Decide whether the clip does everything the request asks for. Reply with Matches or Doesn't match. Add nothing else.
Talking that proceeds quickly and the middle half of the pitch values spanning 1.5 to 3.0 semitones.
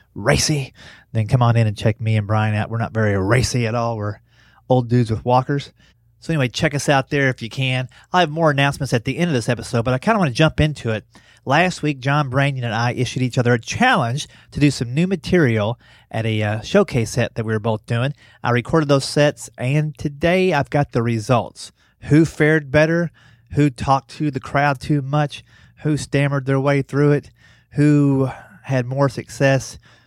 Doesn't match